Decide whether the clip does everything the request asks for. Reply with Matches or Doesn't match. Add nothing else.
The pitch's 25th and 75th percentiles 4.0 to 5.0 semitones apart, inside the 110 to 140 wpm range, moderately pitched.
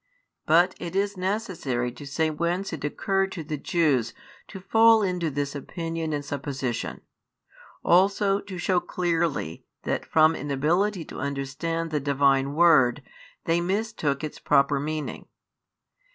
Matches